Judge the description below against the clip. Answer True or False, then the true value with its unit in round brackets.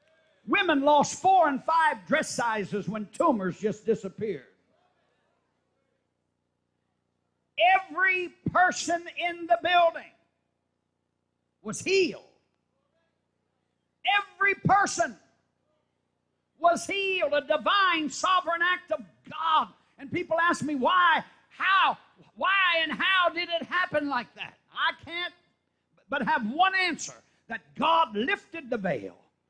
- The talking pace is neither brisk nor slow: False (110 wpm)